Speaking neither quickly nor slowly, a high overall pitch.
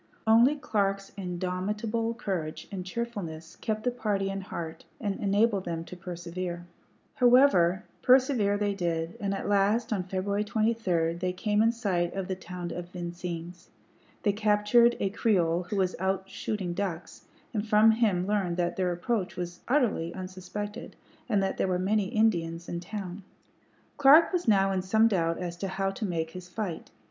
Yes: average, 165 wpm; high, 195 Hz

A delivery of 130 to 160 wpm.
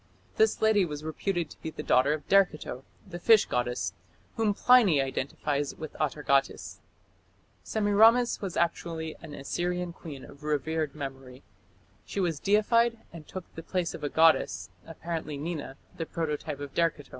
Yes: average, 150 wpm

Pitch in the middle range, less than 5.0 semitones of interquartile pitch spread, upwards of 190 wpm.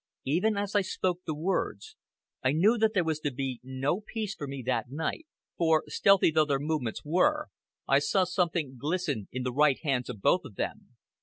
No: medium, 155 Hz; wide, 5.6 semitones; average, 200 wpm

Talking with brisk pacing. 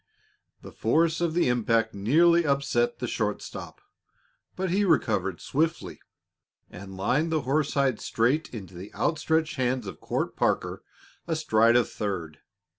No: slow, 135 wpm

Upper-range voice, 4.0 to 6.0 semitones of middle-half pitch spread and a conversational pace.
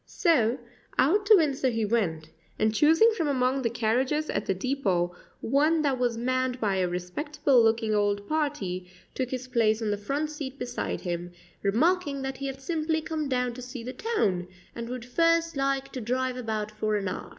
Yes: very high, 255 Hz; average, 5.1 semitones; average, 190 wpm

